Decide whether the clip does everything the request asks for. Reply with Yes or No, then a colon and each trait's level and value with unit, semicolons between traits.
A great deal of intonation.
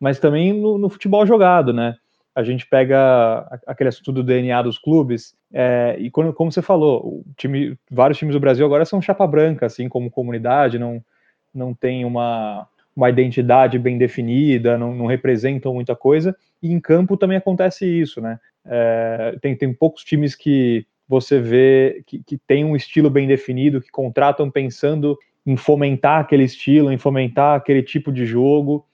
No: average, 3.3 semitones